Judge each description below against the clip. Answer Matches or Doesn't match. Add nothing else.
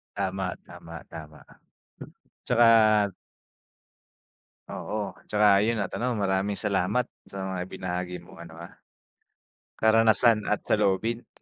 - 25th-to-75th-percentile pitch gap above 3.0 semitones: Doesn't match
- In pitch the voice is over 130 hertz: Doesn't match